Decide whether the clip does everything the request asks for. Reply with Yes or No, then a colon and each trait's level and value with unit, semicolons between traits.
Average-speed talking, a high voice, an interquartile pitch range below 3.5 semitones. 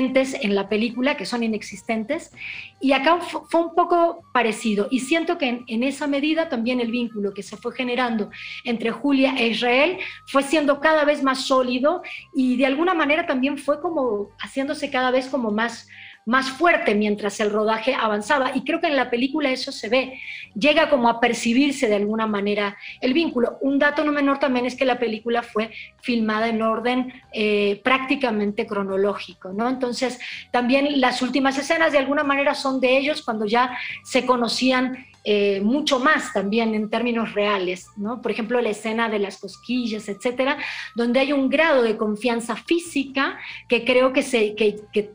No: average, 175 wpm; very high, 250 Hz; average, 4.1 semitones